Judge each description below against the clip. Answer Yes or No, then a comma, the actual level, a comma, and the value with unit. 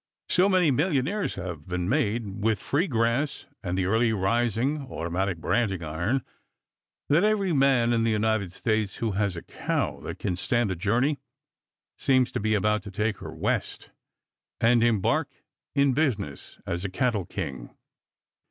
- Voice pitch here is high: No, low, 110 Hz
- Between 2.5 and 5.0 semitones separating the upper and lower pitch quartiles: No, wide, 5.5 semitones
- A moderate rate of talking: Yes, average, 155 wpm